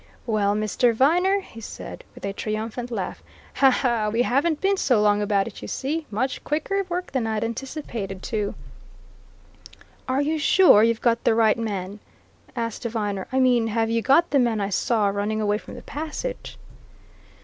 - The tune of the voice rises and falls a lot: No, average, 4.4 semitones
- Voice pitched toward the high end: Yes, high, 230 Hz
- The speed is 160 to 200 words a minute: Yes, average, 170 wpm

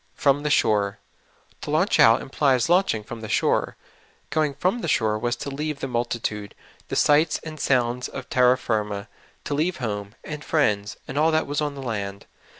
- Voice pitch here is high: No, low, 130 Hz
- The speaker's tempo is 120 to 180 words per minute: No, average, 200 wpm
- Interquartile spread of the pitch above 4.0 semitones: Yes, wide, 5.5 semitones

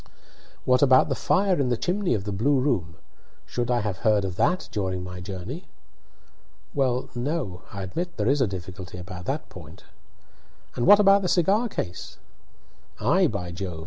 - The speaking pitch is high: No, low, 120 Hz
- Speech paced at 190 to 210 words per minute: No, average, 175 wpm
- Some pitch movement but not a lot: No, wide, 8.2 semitones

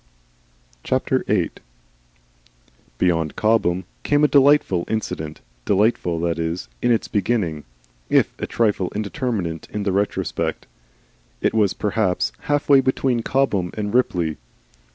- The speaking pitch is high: No, low, 105 Hz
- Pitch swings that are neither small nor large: No, wide, 5.7 semitones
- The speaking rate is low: Yes, slow, 115 wpm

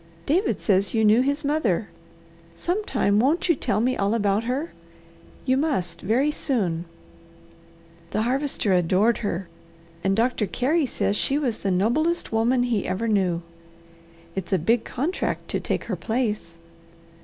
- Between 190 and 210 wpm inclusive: No, average, 145 wpm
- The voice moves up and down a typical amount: No, wide, 5.7 semitones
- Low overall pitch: No, high, 230 Hz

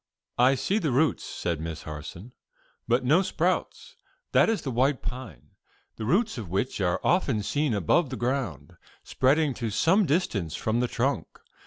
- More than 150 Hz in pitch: No, low, 125 Hz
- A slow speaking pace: No, average, 165 wpm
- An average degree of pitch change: No, wide, 6.9 semitones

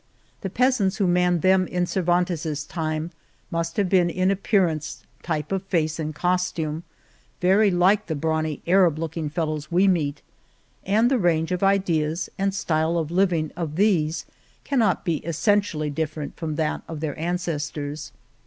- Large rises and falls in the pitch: No, average, 3.1 semitones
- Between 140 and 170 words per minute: Yes, average, 160 wpm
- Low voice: No, medium, 170 Hz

